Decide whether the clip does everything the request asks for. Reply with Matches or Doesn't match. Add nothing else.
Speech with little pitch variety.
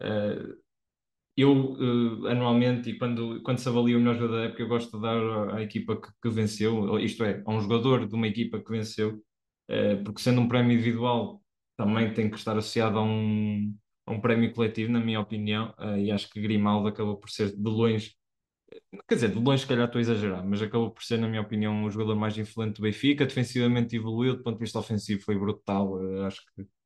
Matches